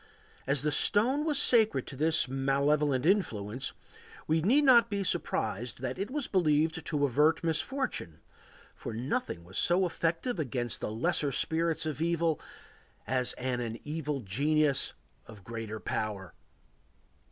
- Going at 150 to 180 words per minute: No, slow, 135 wpm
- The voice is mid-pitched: Yes, medium, 150 Hz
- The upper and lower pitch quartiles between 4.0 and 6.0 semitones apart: Yes, wide, 5.4 semitones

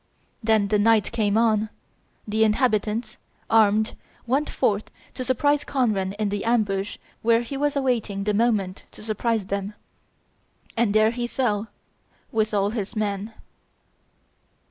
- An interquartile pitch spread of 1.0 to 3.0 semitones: Yes, narrow, 2.4 semitones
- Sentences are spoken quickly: No, slow, 135 wpm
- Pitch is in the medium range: No, high, 215 Hz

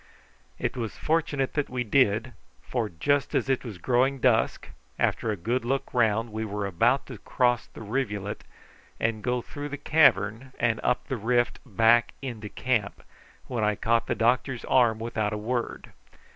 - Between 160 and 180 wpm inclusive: Yes, average, 170 wpm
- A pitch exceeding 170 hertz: No, low, 120 Hz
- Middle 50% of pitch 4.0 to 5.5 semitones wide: No, average, 3.0 semitones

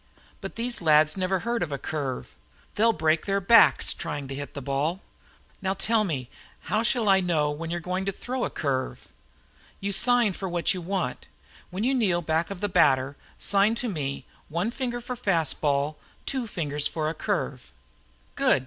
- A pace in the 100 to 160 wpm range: No, average, 185 wpm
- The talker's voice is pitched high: No, medium, 180 Hz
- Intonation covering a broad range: Yes, wide, 6.0 semitones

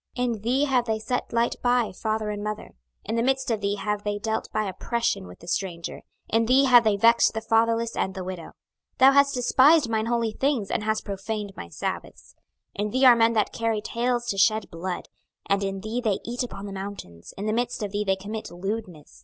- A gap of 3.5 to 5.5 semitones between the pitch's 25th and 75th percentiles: No, average, 2.9 semitones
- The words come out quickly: Yes, fast, 230 wpm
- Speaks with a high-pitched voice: Yes, high, 220 Hz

